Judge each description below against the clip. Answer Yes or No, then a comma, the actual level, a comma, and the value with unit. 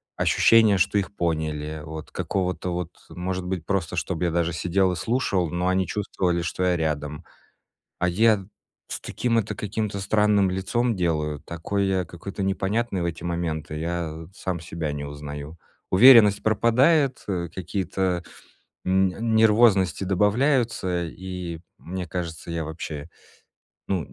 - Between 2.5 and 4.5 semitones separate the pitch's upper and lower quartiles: Yes, average, 3.3 semitones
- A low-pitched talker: Yes, very low, 90 Hz